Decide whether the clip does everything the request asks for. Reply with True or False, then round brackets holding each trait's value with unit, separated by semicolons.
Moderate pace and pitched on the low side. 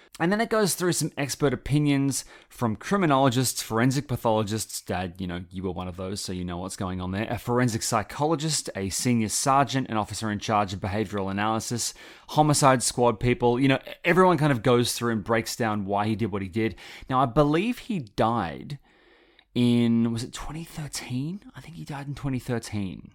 True (190 wpm; 120 Hz)